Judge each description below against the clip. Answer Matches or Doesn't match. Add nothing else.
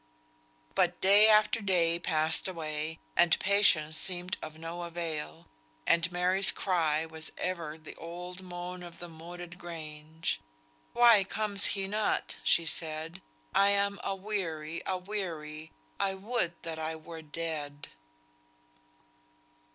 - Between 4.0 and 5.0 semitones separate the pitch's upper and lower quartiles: Doesn't match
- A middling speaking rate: Doesn't match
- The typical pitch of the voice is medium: Matches